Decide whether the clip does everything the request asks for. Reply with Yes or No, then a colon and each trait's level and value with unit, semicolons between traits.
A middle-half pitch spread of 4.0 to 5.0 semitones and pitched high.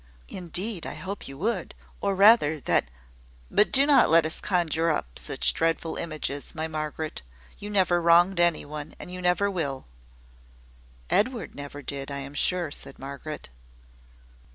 No: average, 4.3 semitones; medium, 165 Hz